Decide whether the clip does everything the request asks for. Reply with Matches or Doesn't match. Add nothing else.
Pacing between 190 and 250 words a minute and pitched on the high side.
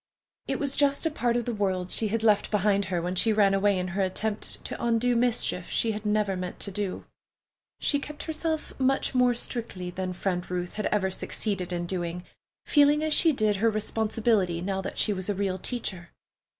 Matches